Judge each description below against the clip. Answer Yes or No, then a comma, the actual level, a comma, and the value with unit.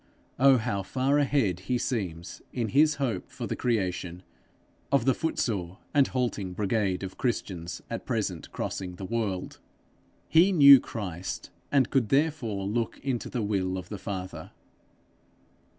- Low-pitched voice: Yes, low, 110 Hz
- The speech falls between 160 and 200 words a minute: No, average, 145 wpm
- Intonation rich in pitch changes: Yes, wide, 6.0 semitones